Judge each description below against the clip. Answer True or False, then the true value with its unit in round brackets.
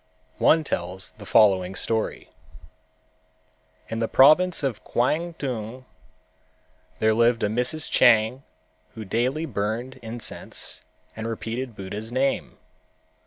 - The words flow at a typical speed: False (105 wpm)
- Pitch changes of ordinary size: True (3.2 semitones)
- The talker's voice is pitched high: False (115 Hz)